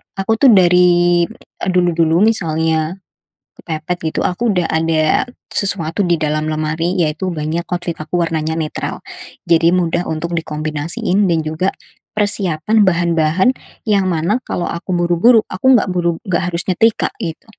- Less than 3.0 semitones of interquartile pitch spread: Yes, narrow, 2.6 semitones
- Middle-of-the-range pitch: Yes, medium, 170 Hz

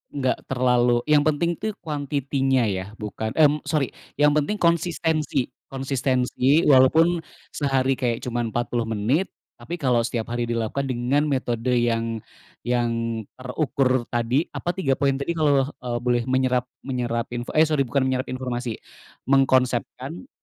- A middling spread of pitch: Yes, average, 3.2 semitones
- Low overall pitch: Yes, low, 130 Hz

